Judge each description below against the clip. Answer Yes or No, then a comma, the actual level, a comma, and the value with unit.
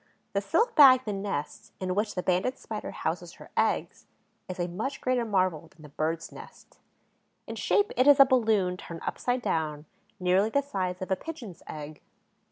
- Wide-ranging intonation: Yes, wide, 6.2 semitones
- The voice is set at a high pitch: Yes, high, 195 Hz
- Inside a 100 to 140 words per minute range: No, average, 180 wpm